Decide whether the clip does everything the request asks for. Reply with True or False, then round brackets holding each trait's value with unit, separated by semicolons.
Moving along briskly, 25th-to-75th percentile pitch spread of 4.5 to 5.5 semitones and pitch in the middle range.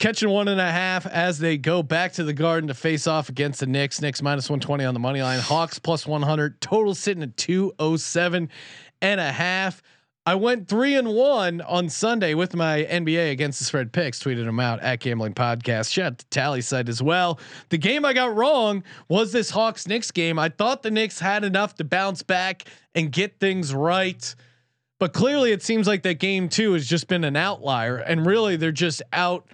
True (210 wpm; 5.1 semitones; 170 Hz)